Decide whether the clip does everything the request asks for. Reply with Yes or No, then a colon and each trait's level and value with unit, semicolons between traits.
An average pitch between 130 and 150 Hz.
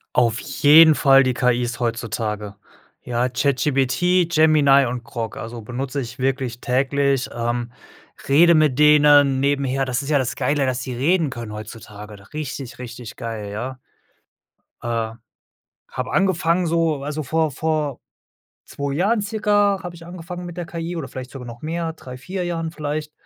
Yes: medium, 140 Hz